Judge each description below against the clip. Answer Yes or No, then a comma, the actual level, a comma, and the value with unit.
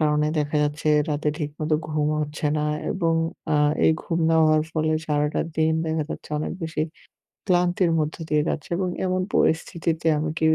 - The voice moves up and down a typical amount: No, narrow, 1.5 semitones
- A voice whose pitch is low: No, medium, 155 Hz